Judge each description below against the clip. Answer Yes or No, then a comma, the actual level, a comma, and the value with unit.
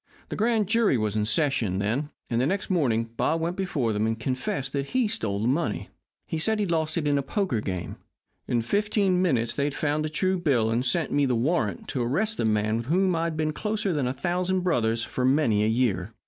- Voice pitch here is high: No, medium, 140 Hz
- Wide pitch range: Yes, wide, 7.7 semitones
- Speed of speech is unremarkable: No, fast, 230 wpm